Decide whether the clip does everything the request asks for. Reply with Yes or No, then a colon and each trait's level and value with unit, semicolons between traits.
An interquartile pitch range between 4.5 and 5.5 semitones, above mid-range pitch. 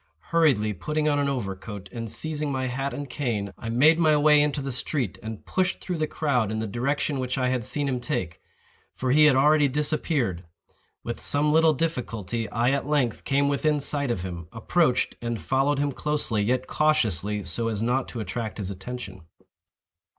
No: average, 5.0 semitones; low, 130 Hz